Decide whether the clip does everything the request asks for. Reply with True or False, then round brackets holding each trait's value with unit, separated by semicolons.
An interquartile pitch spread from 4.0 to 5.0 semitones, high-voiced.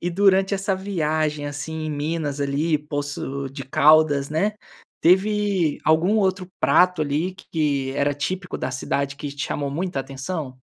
False (4.3 semitones; 155 Hz)